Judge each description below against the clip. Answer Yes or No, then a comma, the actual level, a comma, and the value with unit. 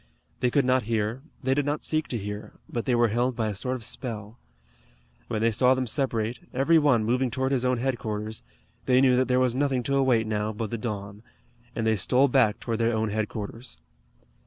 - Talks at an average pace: No, fast, 210 wpm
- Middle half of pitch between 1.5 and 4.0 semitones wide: Yes, average, 3.0 semitones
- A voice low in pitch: Yes, low, 120 Hz